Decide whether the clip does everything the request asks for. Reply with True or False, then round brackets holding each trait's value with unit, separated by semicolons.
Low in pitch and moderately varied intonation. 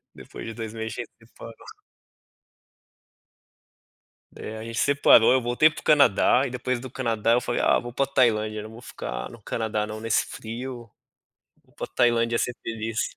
False (115 Hz; 1.8 semitones)